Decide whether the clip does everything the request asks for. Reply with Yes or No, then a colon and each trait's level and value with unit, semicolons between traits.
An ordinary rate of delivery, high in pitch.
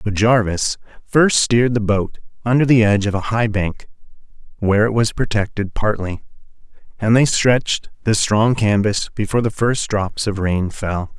No: average, 165 wpm; low, 110 Hz